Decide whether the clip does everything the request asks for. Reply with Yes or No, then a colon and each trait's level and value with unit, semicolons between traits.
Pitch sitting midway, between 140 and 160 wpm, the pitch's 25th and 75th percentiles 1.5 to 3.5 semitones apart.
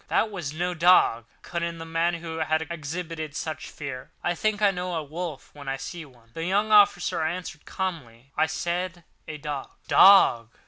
No: medium, 165 Hz; average, 185 wpm; average, 3.2 semitones